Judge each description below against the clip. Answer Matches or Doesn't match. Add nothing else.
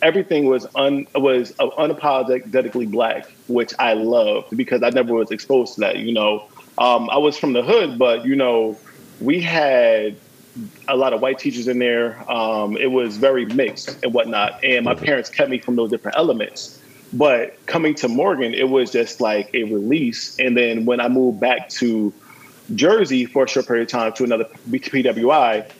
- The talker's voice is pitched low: Matches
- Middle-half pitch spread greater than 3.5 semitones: Doesn't match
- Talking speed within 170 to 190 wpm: Matches